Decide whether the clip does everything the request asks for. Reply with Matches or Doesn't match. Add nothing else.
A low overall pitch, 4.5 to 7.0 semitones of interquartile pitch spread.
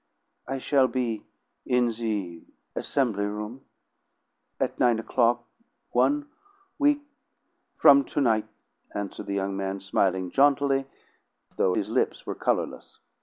Matches